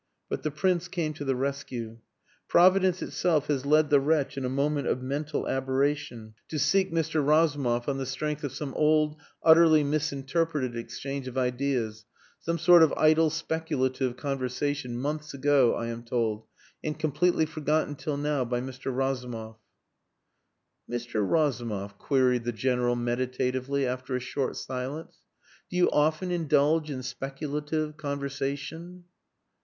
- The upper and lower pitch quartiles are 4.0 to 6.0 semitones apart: No, average, 3.3 semitones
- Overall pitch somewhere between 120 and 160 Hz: Yes, medium, 140 Hz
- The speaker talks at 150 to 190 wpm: No, average, 140 wpm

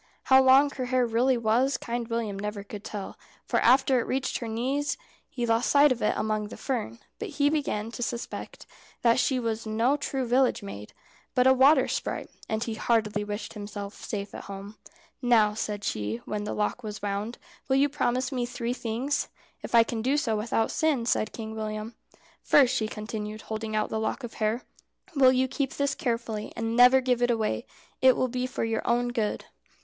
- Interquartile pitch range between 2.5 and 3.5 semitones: Yes, average, 3.1 semitones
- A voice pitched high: Yes, high, 235 Hz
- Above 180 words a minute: Yes, average, 200 wpm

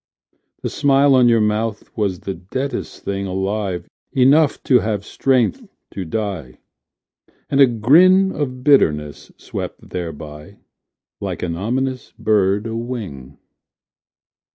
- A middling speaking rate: No, slow, 120 wpm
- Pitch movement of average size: No, wide, 5.9 semitones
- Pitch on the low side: Yes, low, 110 Hz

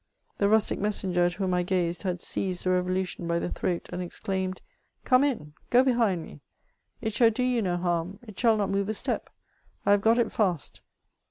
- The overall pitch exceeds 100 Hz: Yes, high, 190 Hz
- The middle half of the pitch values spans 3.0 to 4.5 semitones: Yes, average, 3.6 semitones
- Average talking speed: No, fast, 210 wpm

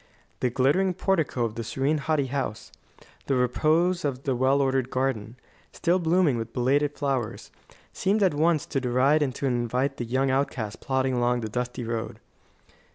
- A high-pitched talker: No, low, 135 Hz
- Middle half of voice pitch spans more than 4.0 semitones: No, average, 3.3 semitones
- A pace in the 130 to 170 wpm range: Yes, average, 165 wpm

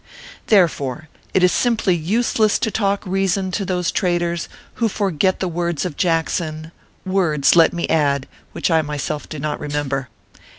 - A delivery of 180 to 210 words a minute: No, average, 155 wpm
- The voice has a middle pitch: Yes, medium, 175 Hz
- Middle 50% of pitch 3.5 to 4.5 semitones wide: Yes, average, 3.8 semitones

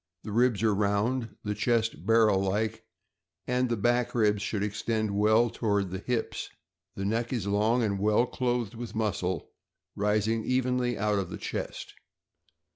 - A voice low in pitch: Yes, low, 110 Hz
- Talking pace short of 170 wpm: Yes, average, 155 wpm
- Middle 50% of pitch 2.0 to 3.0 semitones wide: Yes, average, 2.7 semitones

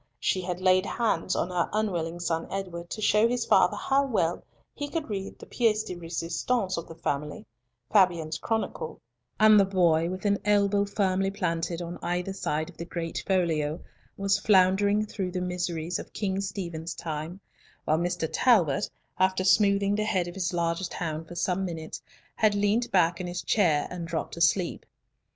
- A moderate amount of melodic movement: Yes, average, 3.1 semitones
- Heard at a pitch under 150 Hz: No, medium, 185 Hz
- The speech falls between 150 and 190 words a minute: Yes, average, 175 wpm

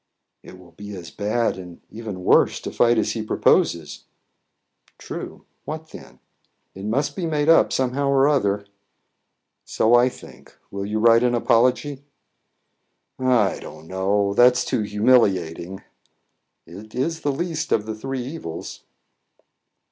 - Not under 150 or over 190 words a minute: No, slow, 135 wpm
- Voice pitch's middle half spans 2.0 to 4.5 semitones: No, average, 5.0 semitones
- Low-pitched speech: Yes, low, 115 Hz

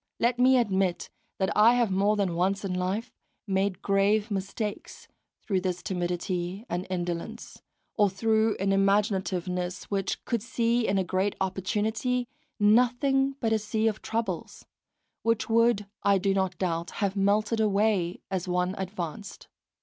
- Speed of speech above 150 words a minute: No, average, 145 wpm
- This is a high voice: Yes, high, 200 Hz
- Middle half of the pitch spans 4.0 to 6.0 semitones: No, average, 2.9 semitones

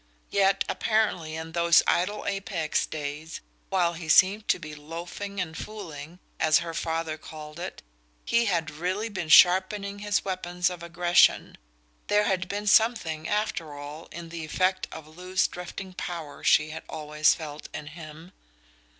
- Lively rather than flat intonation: No, average, 3.4 semitones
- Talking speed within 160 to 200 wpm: No, average, 150 wpm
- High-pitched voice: No, medium, 170 Hz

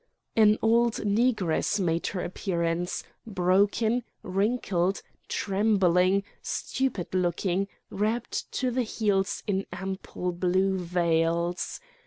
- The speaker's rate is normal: No, slow, 95 wpm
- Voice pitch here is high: Yes, high, 195 Hz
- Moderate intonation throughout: Yes, average, 3.2 semitones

